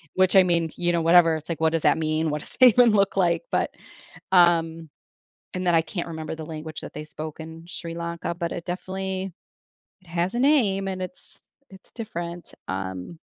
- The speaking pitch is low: No, medium, 170 Hz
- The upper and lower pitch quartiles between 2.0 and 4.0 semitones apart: Yes, narrow, 2.6 semitones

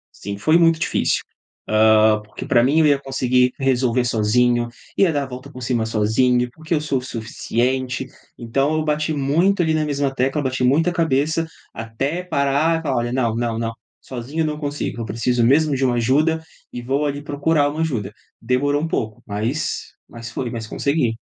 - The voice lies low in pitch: Yes, low, 130 Hz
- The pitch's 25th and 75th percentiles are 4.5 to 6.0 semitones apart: No, average, 4.1 semitones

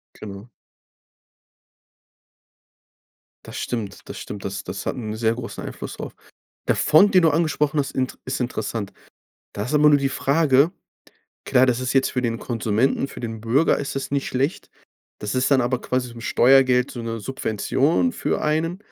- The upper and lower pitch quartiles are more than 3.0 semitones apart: Yes, average, 3.7 semitones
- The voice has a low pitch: Yes, low, 130 Hz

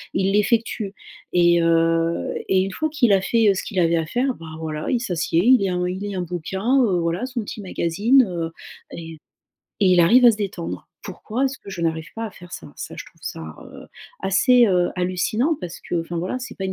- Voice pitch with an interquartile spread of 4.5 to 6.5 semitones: Yes, average, 5.2 semitones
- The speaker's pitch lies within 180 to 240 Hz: Yes, high, 190 Hz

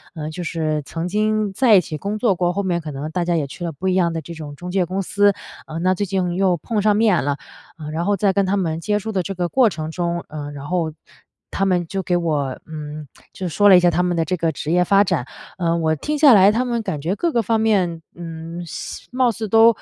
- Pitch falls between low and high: Yes, medium, 180 Hz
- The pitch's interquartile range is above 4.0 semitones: No, average, 3.7 semitones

